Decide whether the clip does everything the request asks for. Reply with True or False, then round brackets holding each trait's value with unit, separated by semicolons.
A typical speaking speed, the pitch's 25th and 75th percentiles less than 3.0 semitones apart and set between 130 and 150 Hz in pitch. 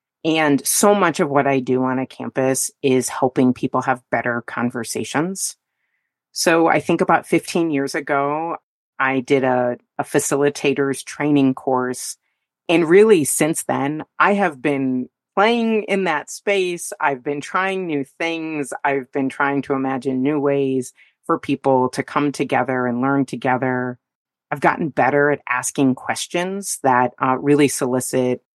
False (150 wpm; 3.8 semitones; 140 Hz)